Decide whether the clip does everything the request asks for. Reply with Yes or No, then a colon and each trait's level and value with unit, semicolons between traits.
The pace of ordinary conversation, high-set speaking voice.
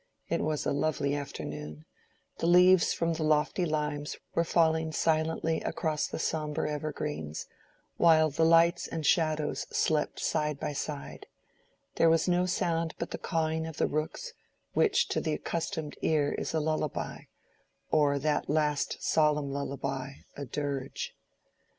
No: average, 145 wpm; medium, 155 Hz